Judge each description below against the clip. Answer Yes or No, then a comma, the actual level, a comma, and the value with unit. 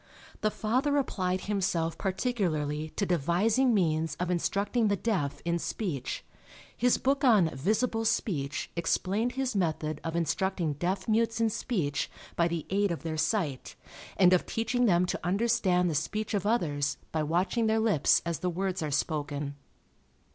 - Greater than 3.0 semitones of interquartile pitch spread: Yes, wide, 5.4 semitones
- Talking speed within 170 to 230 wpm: No, average, 155 wpm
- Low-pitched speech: No, medium, 185 Hz